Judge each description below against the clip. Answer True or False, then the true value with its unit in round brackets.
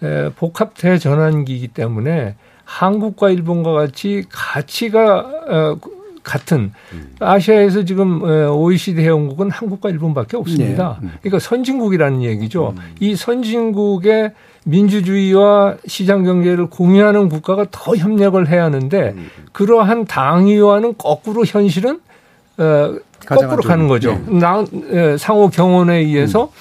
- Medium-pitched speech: True (180 Hz)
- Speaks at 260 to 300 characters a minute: True (280 characters per minute)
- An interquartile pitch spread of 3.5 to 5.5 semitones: True (5.1 semitones)